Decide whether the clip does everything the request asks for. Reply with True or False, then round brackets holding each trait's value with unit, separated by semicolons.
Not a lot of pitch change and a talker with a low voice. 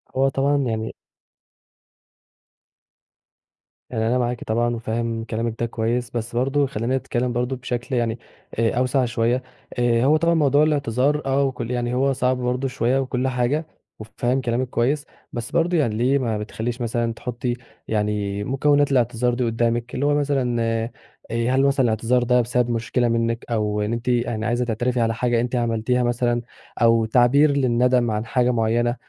True (1.9 semitones; 120 Hz)